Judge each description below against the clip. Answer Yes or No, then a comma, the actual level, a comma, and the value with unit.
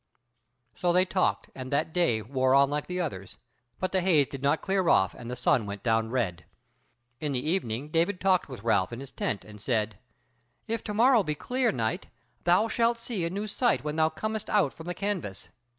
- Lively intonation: Yes, wide, 7.7 semitones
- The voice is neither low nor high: Yes, medium, 155 Hz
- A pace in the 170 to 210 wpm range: Yes, fast, 205 wpm